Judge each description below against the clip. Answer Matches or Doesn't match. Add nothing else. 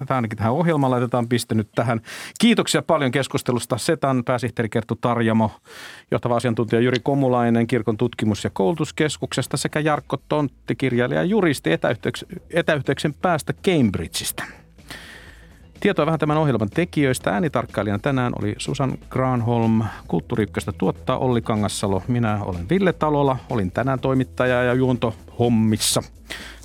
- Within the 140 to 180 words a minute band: Doesn't match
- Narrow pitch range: Doesn't match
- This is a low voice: Matches